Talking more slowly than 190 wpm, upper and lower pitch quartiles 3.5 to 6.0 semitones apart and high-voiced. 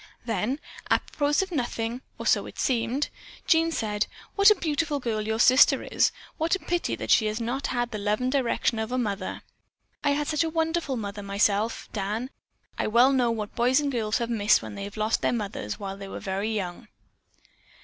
No: average, 200 wpm; average, 5.1 semitones; high, 235 Hz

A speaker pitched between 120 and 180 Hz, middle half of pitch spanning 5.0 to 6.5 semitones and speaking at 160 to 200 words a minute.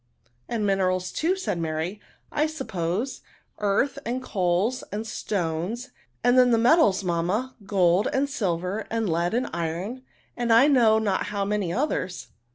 No: high, 205 Hz; wide, 5.6 semitones; average, 165 wpm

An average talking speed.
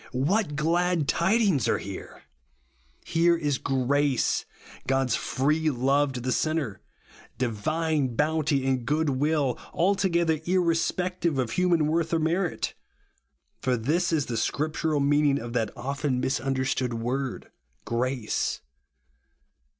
No: slow, 115 wpm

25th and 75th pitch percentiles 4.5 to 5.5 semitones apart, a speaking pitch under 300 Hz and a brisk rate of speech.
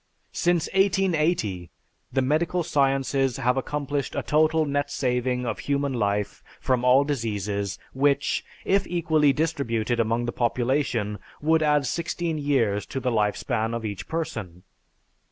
No: average, 4.8 semitones; low, 135 Hz; slow, 135 wpm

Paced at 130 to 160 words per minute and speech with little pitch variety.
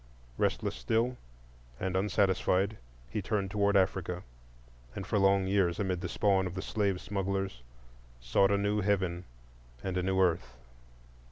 Yes: average, 145 wpm; narrow, 1.7 semitones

